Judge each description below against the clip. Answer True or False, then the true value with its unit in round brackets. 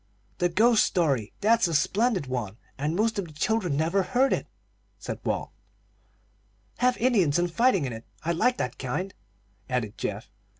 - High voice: False (175 Hz)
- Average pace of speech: True (165 wpm)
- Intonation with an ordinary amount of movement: False (8.1 semitones)